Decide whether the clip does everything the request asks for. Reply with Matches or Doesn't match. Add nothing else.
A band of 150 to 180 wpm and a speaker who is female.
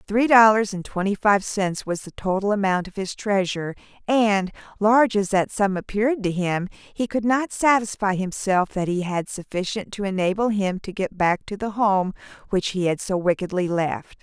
Doesn't match